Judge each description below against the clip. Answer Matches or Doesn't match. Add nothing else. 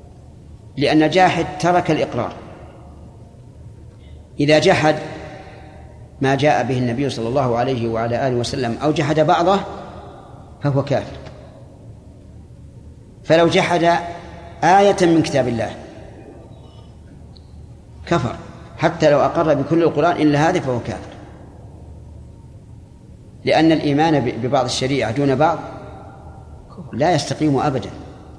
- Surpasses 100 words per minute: Doesn't match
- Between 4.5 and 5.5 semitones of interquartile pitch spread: Matches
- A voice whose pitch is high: Doesn't match